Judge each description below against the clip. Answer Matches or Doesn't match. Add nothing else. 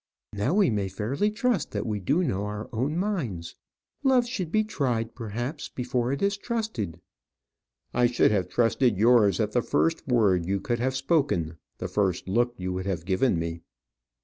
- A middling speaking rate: Matches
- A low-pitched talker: Matches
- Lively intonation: Matches